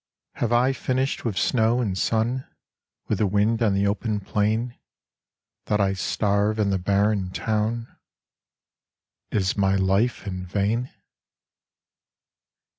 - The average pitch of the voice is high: No, low, 105 Hz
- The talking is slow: Yes, slow, 120 wpm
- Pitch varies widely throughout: No, average, 2.8 semitones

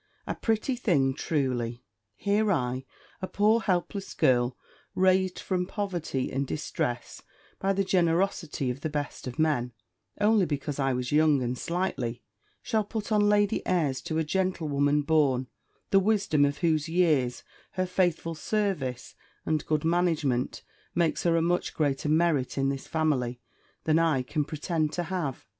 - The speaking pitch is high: No, medium, 160 Hz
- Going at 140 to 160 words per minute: Yes, average, 150 wpm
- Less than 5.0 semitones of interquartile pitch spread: No, wide, 5.4 semitones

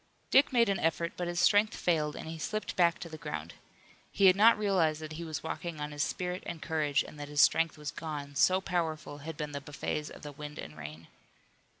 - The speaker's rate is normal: No, fast, 230 wpm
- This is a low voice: No, medium, 160 Hz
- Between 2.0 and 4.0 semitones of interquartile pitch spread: Yes, average, 3.1 semitones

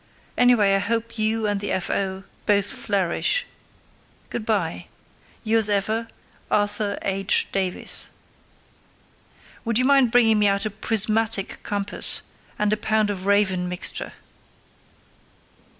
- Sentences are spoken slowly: Yes, slow, 120 wpm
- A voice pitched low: No, high, 205 Hz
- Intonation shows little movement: Yes, narrow, 2.1 semitones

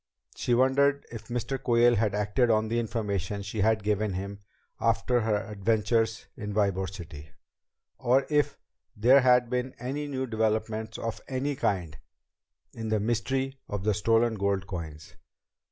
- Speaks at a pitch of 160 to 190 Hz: No, low, 110 Hz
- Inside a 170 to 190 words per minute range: No, average, 150 wpm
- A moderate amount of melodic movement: Yes, average, 3.4 semitones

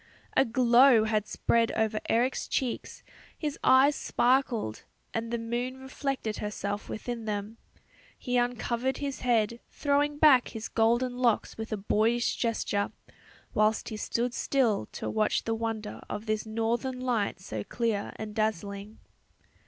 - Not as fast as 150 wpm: Yes, average, 140 wpm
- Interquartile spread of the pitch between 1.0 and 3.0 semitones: Yes, average, 2.7 semitones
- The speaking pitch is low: No, high, 230 Hz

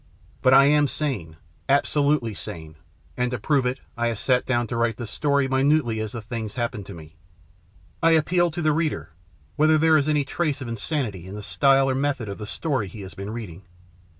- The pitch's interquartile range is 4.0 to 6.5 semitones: Yes, average, 5.1 semitones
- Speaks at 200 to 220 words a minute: Yes, fast, 205 wpm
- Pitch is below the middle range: Yes, low, 130 Hz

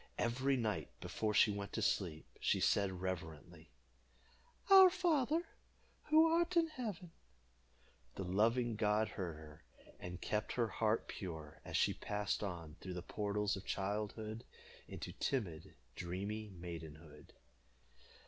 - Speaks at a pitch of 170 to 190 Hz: No, low, 105 Hz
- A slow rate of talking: Yes, slow, 130 wpm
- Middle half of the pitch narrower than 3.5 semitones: No, average, 5.2 semitones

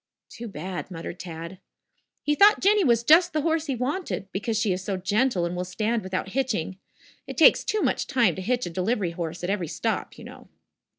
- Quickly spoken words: Yes, fast, 210 wpm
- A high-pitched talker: Yes, high, 205 Hz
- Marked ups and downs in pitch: Yes, wide, 6.4 semitones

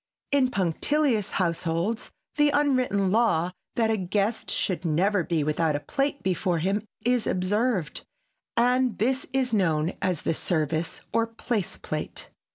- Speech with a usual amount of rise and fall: No, wide, 6.3 semitones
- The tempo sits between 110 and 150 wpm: Yes, average, 140 wpm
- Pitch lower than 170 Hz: No, high, 200 Hz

